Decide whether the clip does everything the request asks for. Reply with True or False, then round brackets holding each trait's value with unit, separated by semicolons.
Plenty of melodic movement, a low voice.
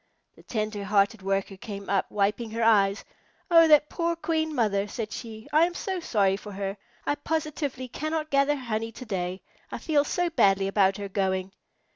False (7.0 semitones; 220 Hz)